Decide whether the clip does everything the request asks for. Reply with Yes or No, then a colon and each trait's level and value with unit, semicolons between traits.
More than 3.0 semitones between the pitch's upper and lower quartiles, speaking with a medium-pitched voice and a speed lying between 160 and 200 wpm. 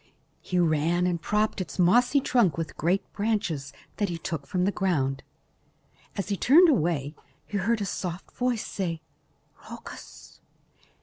No: average, 4.2 semitones; medium, 180 Hz; average, 150 wpm